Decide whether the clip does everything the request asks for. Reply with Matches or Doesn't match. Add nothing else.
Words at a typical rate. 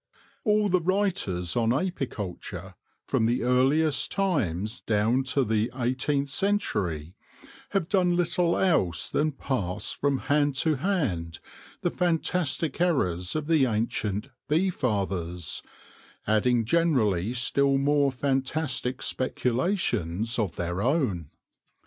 Doesn't match